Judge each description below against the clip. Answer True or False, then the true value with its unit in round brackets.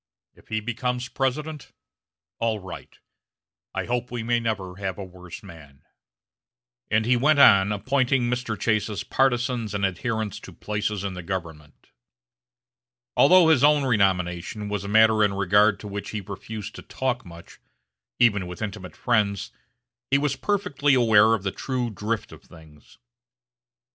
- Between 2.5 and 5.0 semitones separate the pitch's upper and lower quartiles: True (4.1 semitones)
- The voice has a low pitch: True (110 Hz)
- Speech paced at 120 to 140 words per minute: False (150 wpm)